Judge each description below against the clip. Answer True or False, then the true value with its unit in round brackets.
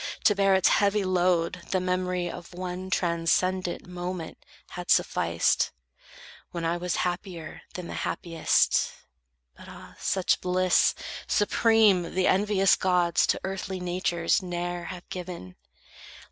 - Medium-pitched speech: True (180 Hz)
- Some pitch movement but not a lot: False (1.3 semitones)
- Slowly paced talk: True (125 wpm)